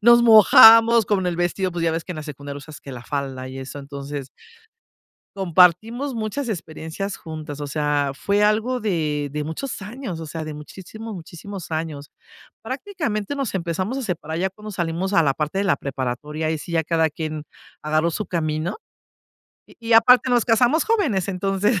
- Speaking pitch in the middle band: Yes, medium, 175 Hz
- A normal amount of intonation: No, wide, 6.0 semitones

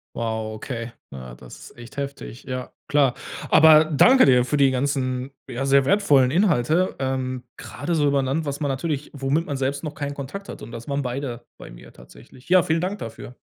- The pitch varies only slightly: No, average, 3.0 semitones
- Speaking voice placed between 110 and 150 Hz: Yes, low, 135 Hz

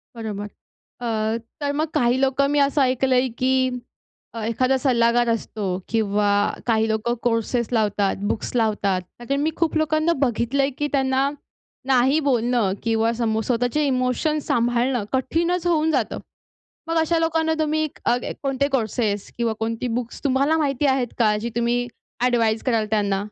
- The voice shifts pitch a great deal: No, average, 3.7 semitones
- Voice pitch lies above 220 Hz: Yes, high, 245 Hz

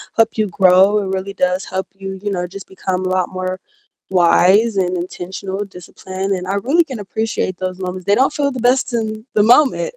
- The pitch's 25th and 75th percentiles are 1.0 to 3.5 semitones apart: Yes, average, 2.9 semitones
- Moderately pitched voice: No, high, 195 Hz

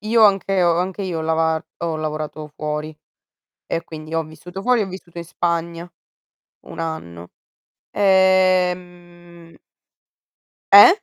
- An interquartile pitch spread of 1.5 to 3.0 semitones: Yes, narrow, 2.6 semitones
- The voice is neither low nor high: Yes, medium, 170 Hz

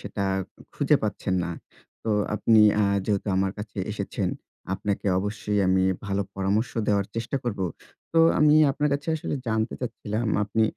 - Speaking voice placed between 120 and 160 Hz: No, low, 105 Hz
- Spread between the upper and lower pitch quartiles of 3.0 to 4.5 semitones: No, narrow, 2.5 semitones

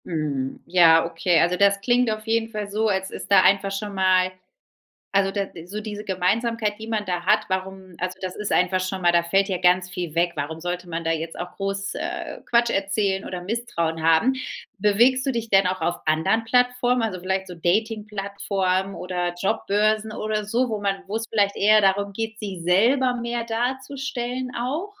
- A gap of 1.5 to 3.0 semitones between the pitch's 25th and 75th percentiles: No, average, 3.5 semitones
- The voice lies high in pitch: Yes, high, 195 Hz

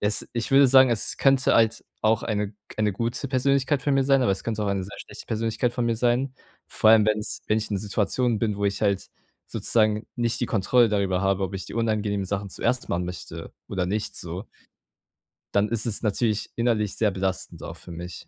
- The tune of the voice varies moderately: Yes, average, 3.0 semitones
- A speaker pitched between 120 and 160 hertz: No, low, 110 Hz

